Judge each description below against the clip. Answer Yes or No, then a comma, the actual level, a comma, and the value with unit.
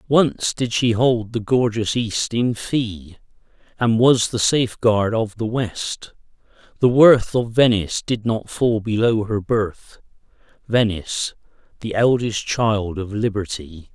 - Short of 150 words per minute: Yes, average, 140 wpm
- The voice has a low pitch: Yes, low, 110 Hz